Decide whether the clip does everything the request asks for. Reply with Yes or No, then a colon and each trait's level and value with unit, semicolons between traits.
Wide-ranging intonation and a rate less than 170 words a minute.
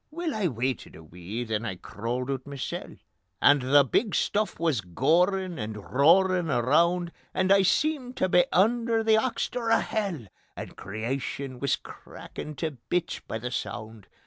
Yes: wide, 8.0 semitones; average, 160 wpm